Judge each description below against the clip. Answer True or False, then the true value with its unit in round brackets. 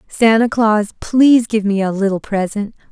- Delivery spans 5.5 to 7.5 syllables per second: False (4.8 syllables/s)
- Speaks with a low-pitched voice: False (215 Hz)